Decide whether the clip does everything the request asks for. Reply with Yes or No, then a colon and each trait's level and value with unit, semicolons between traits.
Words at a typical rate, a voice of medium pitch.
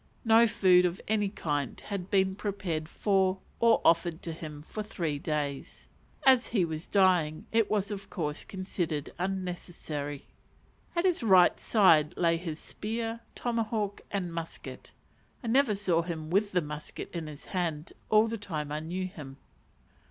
Yes: average, 155 wpm; medium, 180 Hz